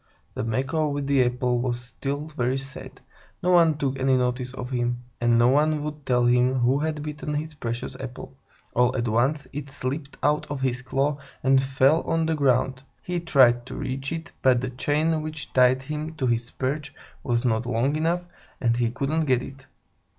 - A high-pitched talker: No, low, 135 Hz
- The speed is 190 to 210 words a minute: Yes, average, 195 wpm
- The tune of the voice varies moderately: Yes, average, 3.2 semitones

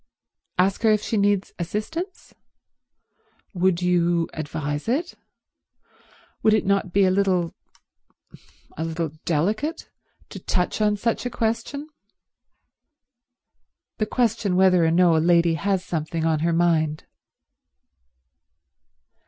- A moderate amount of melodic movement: Yes, average, 4.2 semitones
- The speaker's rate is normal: No, slow, 110 wpm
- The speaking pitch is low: No, medium, 185 Hz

